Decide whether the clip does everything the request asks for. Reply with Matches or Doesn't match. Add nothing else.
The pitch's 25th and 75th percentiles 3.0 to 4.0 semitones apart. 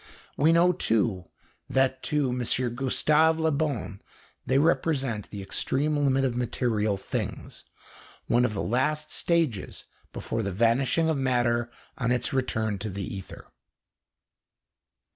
Doesn't match